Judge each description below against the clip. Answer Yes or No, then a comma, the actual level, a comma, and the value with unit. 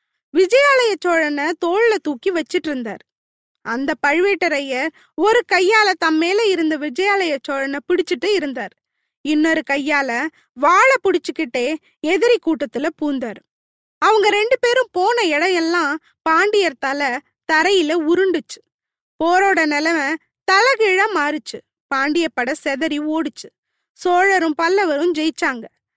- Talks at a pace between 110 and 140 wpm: No, average, 100 wpm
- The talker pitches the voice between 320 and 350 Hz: Yes, very high, 330 Hz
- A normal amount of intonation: Yes, average, 4.4 semitones